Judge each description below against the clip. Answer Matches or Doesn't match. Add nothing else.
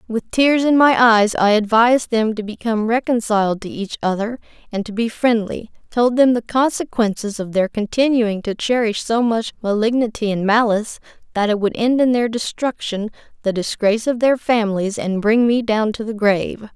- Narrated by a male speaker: Doesn't match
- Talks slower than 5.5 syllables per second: Matches